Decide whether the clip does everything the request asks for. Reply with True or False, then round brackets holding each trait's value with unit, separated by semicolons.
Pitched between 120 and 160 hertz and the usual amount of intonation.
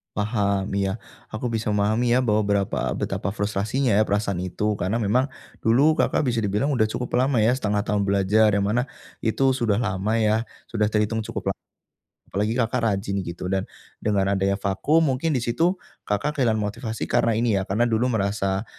False (110 Hz; 3.0 semitones)